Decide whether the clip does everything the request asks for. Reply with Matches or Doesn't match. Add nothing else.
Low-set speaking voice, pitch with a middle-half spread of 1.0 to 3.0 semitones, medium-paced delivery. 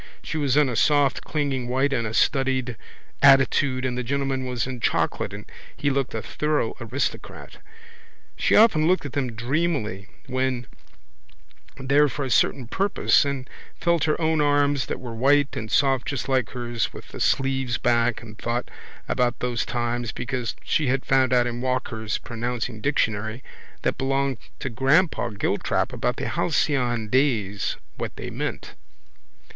Matches